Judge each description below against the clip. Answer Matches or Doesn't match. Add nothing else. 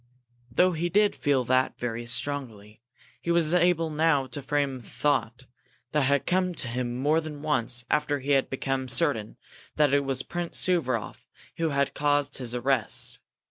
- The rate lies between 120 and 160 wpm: Doesn't match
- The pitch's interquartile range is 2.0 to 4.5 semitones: Matches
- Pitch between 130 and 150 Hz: Matches